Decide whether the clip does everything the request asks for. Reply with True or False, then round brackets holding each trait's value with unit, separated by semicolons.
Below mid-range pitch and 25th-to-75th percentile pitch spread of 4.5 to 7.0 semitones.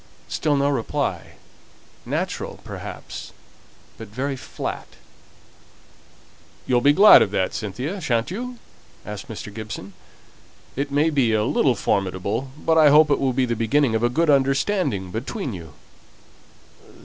True (130 Hz; 5.2 semitones)